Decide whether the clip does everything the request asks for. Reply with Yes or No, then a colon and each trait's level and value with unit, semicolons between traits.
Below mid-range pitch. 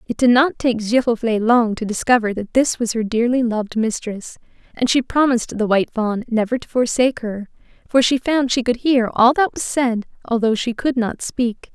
No: high, 235 Hz